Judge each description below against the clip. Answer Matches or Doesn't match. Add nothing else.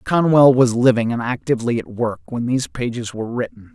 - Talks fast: Doesn't match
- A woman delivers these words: Doesn't match